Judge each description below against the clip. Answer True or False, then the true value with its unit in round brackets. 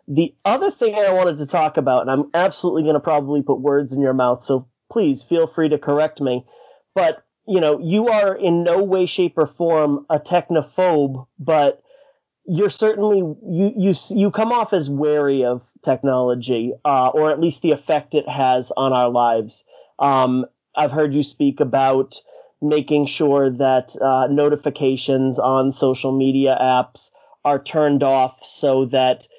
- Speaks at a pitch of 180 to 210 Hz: False (145 Hz)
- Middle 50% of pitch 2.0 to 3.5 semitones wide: False (4.4 semitones)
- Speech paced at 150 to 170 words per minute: True (165 wpm)